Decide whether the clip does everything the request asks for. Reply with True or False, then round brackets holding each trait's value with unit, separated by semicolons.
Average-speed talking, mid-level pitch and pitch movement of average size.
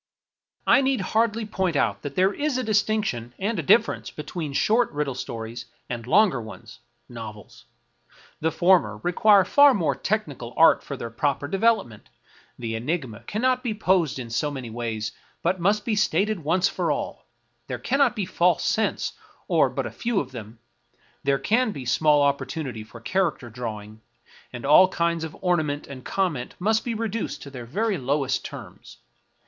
False (170 wpm; 160 Hz; 9.0 semitones)